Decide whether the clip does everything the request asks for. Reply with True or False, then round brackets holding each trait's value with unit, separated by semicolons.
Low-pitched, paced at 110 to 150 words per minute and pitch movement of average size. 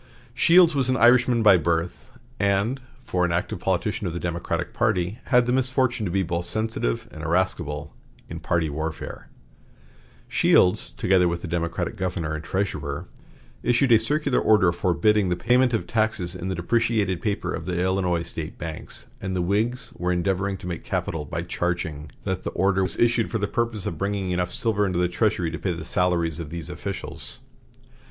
False (95 Hz; 180 wpm; 4.3 semitones)